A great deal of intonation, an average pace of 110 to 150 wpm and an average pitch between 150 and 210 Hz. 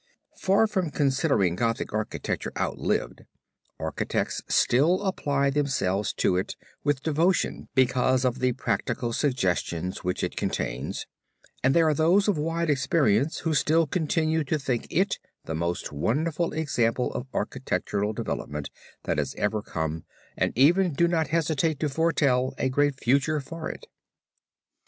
No: wide, 5.7 semitones; average, 140 wpm; medium, 140 Hz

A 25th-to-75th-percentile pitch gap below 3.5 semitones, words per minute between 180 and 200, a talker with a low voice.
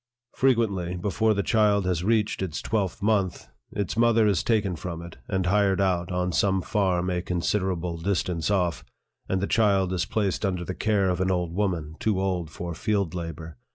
Yes: average, 2.7 semitones; average, 185 wpm; very low, 95 Hz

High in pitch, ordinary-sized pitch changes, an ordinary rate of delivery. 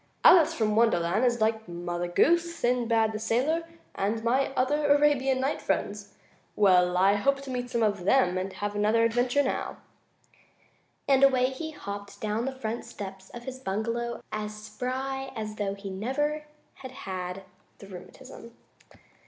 Yes: high, 230 Hz; average, 4.5 semitones; average, 155 wpm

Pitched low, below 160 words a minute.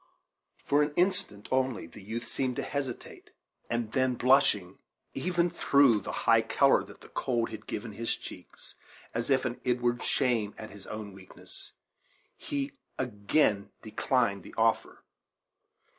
Yes: low, 120 Hz; average, 145 wpm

